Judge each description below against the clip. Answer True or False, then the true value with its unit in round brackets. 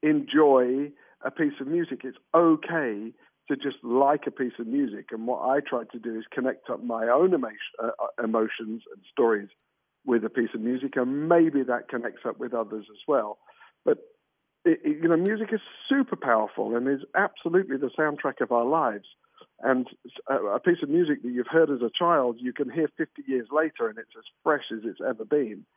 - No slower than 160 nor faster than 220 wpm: True (200 wpm)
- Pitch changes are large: True (5.7 semitones)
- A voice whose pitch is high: False (140 Hz)